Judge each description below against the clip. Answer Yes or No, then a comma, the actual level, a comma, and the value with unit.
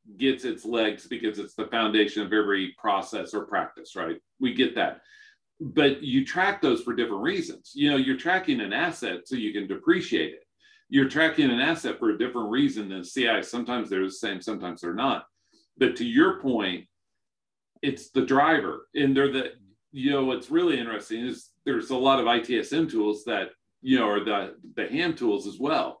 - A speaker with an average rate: Yes, average, 190 wpm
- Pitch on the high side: No, medium, 140 Hz